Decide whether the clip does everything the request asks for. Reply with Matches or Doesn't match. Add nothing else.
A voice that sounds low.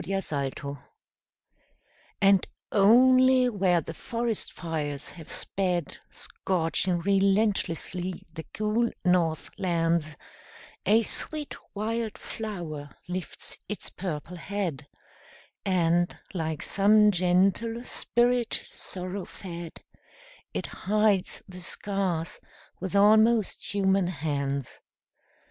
Doesn't match